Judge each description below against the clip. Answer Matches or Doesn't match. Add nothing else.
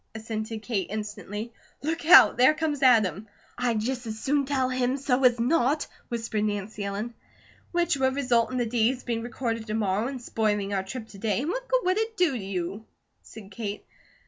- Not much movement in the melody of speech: Doesn't match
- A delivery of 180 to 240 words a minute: Matches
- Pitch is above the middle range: Matches